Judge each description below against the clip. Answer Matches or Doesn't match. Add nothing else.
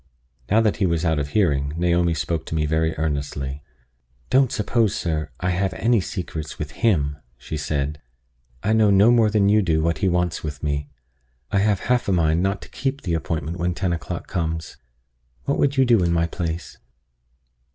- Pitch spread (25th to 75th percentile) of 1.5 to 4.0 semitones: Doesn't match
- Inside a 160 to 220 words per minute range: Matches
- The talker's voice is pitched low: Matches